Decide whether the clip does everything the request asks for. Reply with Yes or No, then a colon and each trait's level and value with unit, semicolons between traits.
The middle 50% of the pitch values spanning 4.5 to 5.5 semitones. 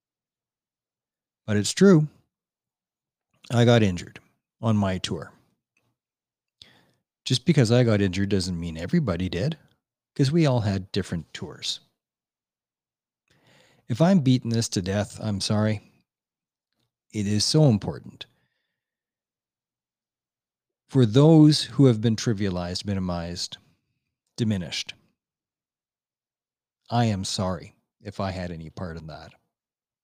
Yes: average, 5.0 semitones